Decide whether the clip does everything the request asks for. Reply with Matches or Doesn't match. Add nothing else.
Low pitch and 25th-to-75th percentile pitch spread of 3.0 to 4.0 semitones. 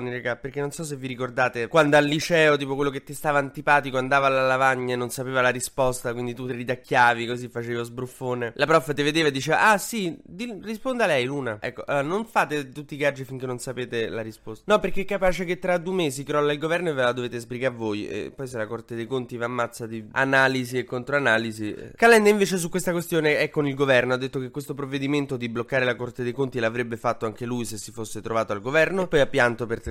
Matches